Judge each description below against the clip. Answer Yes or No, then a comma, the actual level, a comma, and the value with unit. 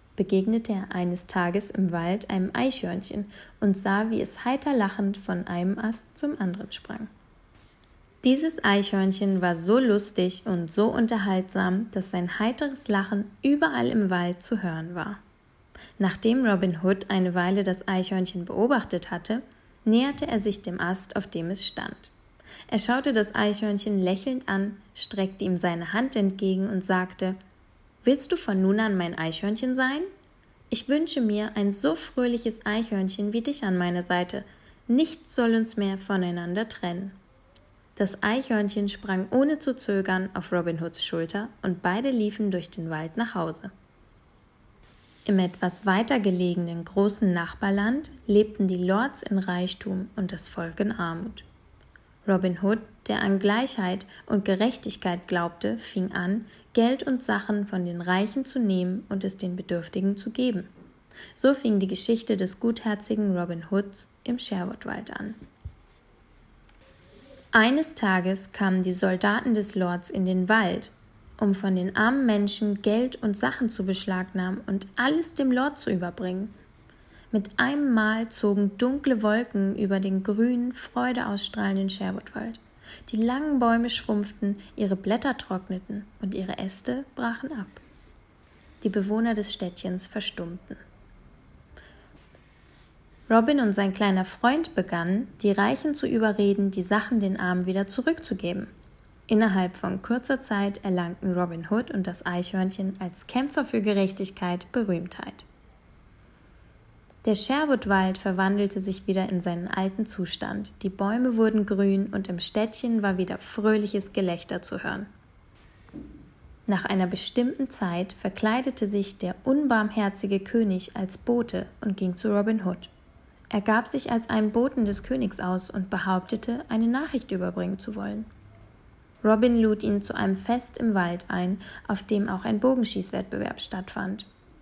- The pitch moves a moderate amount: Yes, average, 3.3 semitones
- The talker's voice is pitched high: Yes, high, 200 Hz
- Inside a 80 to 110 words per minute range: No, fast, 140 wpm